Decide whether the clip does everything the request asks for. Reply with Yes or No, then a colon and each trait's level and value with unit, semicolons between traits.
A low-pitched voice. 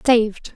No: high, 225 Hz